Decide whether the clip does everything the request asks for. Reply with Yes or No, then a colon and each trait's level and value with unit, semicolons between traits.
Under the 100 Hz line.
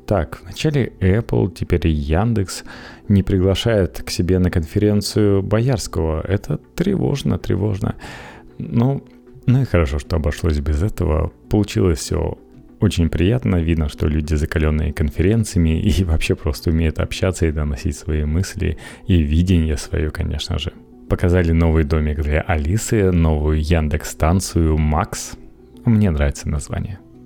Yes: very low, 90 Hz